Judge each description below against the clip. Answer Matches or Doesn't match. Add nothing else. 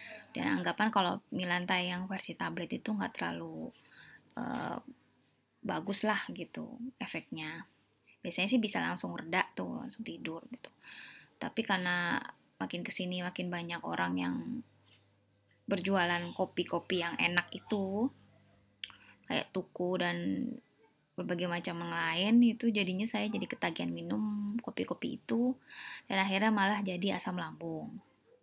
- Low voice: Doesn't match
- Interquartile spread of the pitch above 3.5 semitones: Matches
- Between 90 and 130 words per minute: Matches